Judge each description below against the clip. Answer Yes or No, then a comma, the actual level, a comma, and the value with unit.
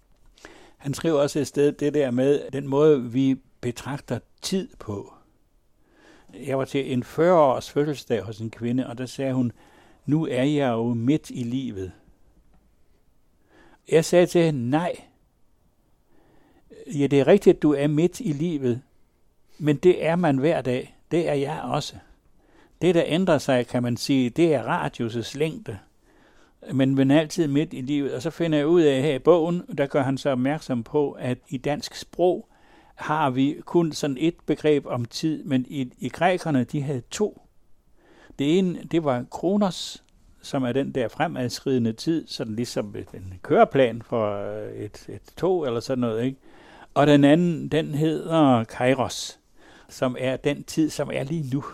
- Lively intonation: No, average, 3.7 semitones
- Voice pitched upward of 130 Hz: Yes, medium, 140 Hz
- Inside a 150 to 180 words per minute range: Yes, average, 170 wpm